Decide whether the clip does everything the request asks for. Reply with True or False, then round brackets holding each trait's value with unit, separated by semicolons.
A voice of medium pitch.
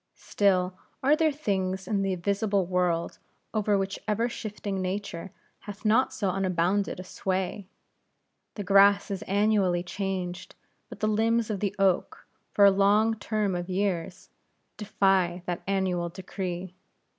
False (195 Hz)